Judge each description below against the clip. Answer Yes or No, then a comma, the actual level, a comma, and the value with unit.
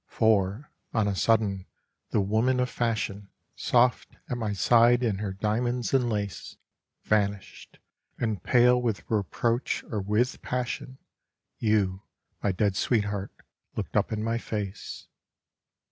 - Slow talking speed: Yes, slow, 130 wpm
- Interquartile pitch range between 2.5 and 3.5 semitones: Yes, average, 3.1 semitones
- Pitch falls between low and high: No, low, 110 Hz